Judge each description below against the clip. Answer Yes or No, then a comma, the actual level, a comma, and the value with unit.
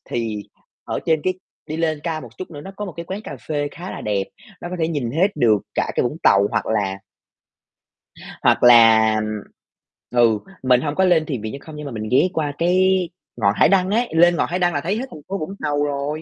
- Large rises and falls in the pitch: Yes, wide, 7.0 semitones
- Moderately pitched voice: Yes, medium, 150 Hz